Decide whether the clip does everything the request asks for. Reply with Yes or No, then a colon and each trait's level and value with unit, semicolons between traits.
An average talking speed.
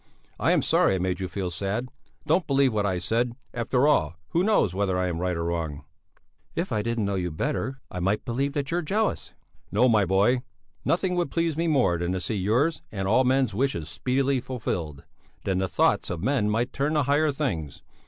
No: fast, 210 wpm